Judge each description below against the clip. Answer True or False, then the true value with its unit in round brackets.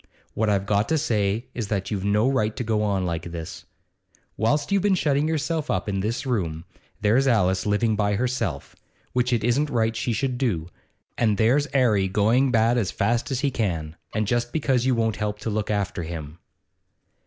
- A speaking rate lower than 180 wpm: False (200 wpm)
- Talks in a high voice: False (110 Hz)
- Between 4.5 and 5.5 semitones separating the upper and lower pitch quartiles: False (3.9 semitones)